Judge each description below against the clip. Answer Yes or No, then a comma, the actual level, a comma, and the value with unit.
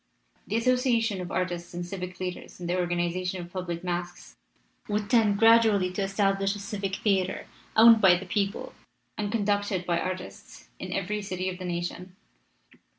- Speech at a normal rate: Yes, average, 170 wpm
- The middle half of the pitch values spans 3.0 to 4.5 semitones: No, narrow, 2.4 semitones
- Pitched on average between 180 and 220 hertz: Yes, high, 190 Hz